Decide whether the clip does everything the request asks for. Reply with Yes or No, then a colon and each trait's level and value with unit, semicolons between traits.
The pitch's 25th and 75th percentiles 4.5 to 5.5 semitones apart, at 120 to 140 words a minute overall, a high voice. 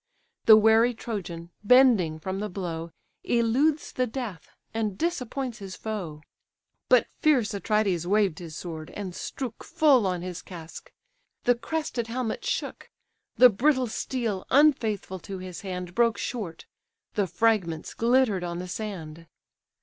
Yes: average, 5.2 semitones; slow, 135 wpm; high, 210 Hz